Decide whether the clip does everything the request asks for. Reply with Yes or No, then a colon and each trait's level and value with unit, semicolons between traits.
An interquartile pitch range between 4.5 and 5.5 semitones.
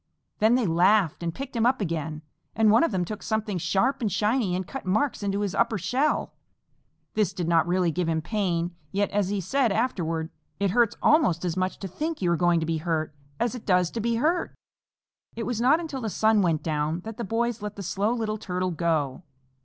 Yes: average, 5.0 semitones